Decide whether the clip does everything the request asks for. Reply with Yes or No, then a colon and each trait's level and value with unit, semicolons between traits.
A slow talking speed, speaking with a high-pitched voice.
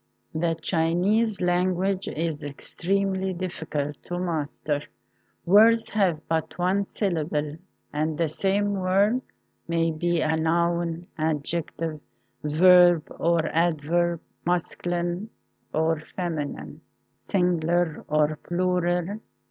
No: slow, 100 wpm; medium, 170 Hz